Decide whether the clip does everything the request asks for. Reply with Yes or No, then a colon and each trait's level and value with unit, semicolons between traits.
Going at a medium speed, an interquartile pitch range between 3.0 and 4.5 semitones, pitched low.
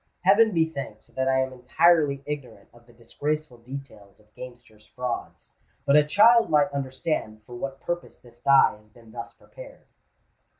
Yes: average, 165 wpm; average, 4.2 semitones; low, 130 Hz